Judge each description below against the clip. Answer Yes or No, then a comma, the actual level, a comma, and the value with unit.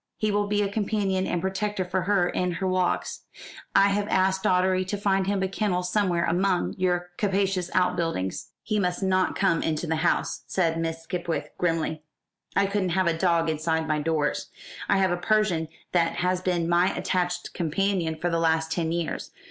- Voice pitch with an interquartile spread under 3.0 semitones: Yes, narrow, 2.6 semitones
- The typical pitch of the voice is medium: Yes, medium, 180 Hz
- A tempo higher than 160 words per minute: Yes, average, 185 wpm